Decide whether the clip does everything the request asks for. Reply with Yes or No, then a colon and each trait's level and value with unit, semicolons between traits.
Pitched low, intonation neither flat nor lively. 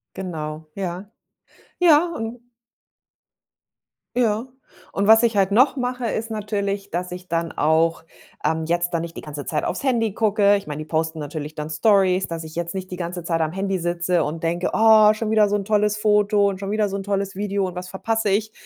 No: high, 195 Hz; average, 4.0 semitones